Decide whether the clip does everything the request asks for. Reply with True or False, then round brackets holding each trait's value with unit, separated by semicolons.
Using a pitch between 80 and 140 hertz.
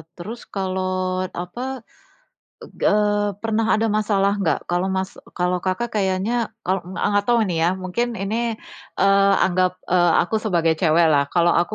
False (190 Hz)